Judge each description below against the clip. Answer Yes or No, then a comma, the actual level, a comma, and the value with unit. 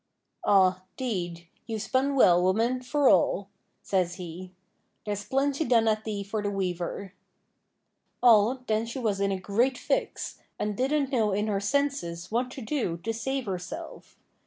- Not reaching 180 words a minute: Yes, average, 160 wpm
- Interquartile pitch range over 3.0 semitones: Yes, average, 5.0 semitones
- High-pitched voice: Yes, high, 215 Hz